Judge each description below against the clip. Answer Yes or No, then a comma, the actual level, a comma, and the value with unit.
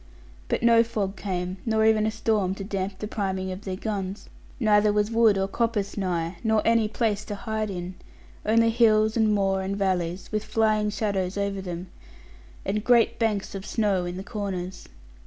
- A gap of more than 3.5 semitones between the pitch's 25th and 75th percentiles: No, narrow, 2.4 semitones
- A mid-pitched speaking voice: No, high, 205 Hz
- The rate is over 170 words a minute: Yes, average, 180 wpm